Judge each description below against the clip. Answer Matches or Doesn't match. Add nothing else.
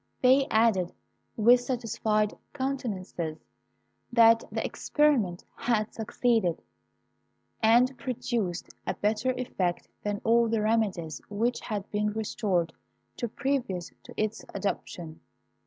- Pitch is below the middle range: Doesn't match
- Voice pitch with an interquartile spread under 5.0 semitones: Matches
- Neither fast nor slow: Doesn't match